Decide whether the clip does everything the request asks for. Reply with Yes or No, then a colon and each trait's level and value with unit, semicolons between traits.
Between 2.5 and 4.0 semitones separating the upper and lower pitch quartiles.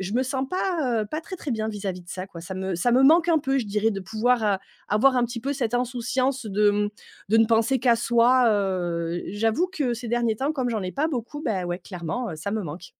No: average, 4.7 semitones